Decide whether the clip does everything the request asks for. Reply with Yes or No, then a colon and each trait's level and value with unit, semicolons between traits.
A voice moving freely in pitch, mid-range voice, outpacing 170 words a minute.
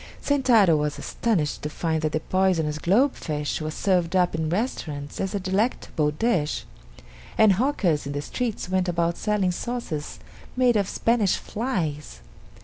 No: wide, 5.9 semitones; medium, 180 Hz; average, 150 wpm